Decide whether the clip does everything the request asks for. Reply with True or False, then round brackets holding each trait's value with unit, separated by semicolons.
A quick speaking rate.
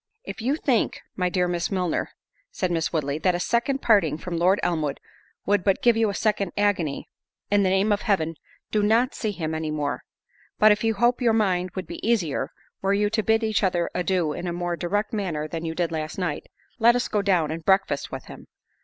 True (215 wpm)